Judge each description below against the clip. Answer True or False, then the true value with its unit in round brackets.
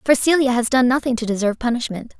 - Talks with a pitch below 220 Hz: False (245 Hz)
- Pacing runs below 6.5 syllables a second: False (6.7 syllables/s)